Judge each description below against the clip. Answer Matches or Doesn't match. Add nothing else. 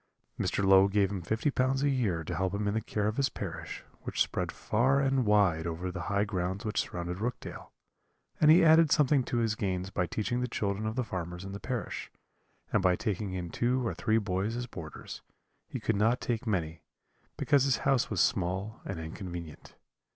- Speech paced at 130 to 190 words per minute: Doesn't match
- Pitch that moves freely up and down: Doesn't match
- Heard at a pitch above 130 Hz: Doesn't match